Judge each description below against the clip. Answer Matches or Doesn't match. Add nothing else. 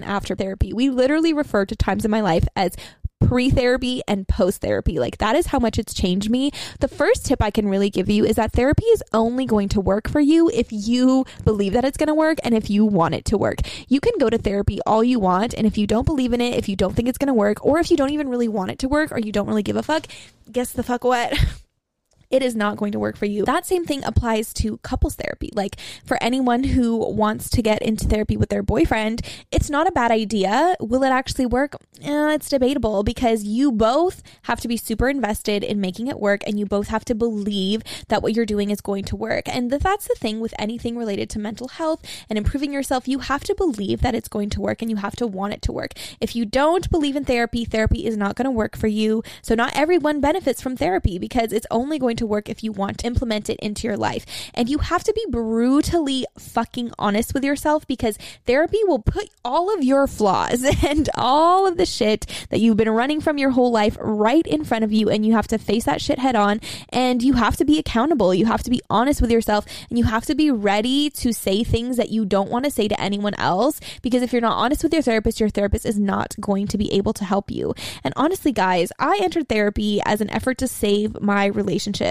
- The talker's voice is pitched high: Matches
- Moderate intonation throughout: Matches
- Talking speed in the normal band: Doesn't match